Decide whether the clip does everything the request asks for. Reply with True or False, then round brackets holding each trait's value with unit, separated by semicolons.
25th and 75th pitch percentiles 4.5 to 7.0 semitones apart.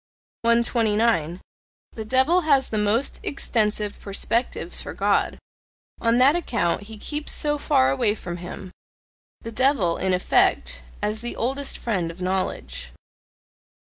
True (5.6 semitones)